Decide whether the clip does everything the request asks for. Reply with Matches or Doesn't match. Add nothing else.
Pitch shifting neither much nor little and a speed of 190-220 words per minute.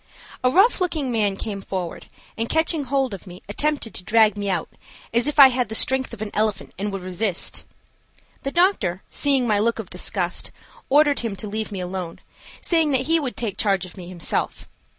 Doesn't match